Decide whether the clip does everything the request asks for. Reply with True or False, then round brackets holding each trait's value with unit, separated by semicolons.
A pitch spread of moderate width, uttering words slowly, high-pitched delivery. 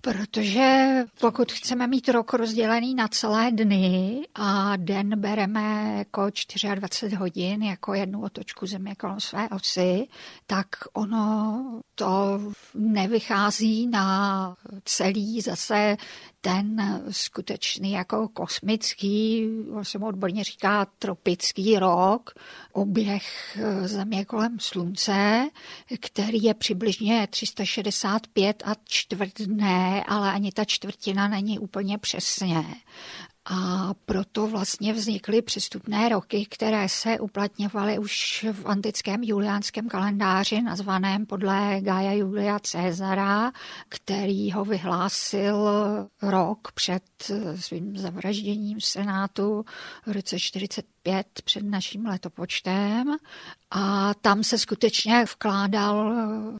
False (1.8 semitones; 100 wpm; 205 Hz)